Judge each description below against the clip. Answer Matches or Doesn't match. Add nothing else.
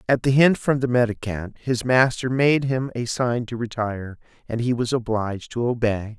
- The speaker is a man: Matches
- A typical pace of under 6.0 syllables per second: Matches